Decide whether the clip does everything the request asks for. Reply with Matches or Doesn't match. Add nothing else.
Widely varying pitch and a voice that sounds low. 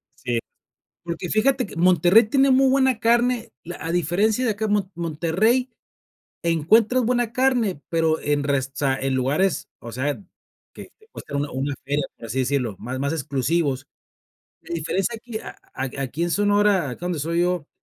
Doesn't match